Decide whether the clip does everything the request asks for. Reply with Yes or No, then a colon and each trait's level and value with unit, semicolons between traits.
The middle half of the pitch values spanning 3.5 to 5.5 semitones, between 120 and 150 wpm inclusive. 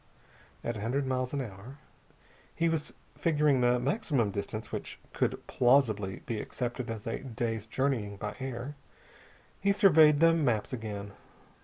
Yes: average, 4.6 semitones; average, 145 wpm